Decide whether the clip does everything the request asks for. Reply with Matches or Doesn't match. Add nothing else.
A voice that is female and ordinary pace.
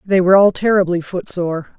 Matches